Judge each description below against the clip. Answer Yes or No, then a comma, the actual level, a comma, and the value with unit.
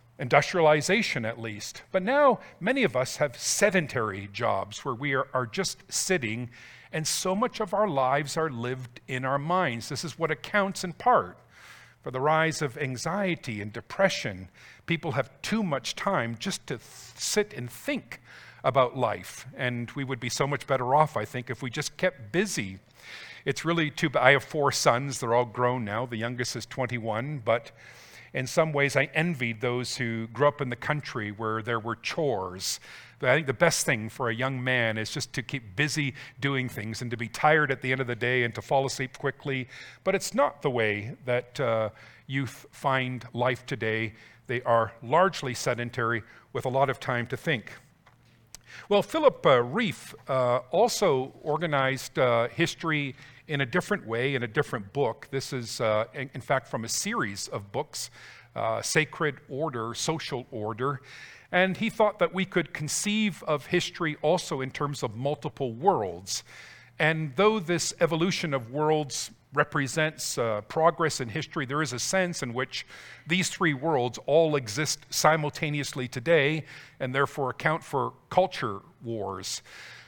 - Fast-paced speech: No, average, 175 wpm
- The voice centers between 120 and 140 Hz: Yes, low, 135 Hz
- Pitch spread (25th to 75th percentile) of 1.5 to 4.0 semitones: No, average, 4.5 semitones